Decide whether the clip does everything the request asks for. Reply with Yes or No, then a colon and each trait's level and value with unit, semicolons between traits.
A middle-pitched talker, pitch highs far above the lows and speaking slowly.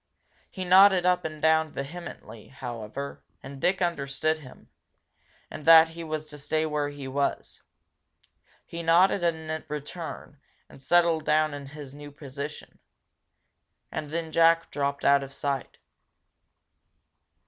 No: medium, 155 Hz; average, 2.8 semitones; slow, 130 wpm